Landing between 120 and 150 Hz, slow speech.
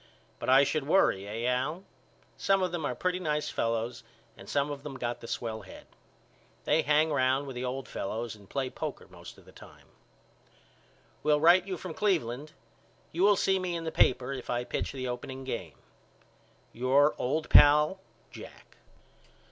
No: medium, 140 Hz; average, 170 wpm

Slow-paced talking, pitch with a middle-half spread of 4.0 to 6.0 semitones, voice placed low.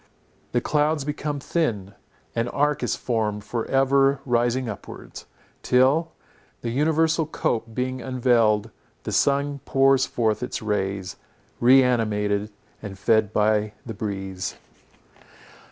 Yes: slow, 120 wpm; average, 4.4 semitones; low, 120 Hz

